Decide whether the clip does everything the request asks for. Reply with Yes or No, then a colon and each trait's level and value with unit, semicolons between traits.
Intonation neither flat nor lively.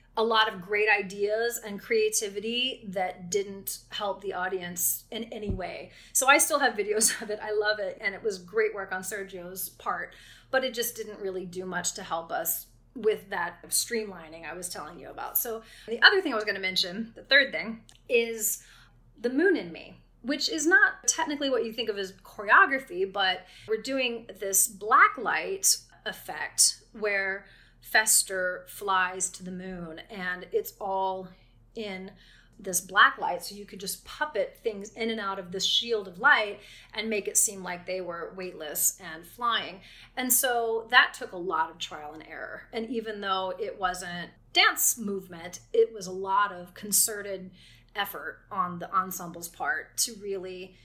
Yes: average, 4.0 semitones